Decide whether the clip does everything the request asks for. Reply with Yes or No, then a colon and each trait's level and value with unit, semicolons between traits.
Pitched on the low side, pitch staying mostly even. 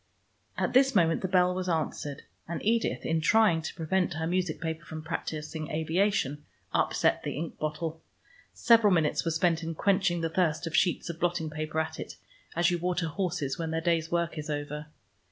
No: medium, 165 Hz; narrow, 2.1 semitones